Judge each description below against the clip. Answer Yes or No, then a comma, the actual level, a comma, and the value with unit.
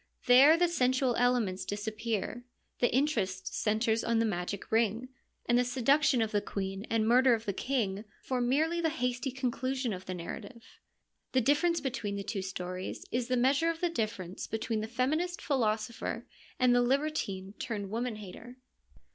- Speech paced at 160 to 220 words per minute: Yes, average, 170 wpm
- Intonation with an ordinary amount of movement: Yes, average, 3.7 semitones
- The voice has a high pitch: Yes, high, 240 Hz